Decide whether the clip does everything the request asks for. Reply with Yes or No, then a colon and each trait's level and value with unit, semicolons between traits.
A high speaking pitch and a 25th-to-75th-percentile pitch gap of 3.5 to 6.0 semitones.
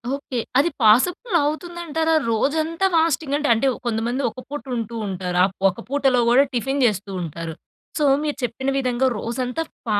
Yes: very high, 265 Hz; average, 4.8 semitones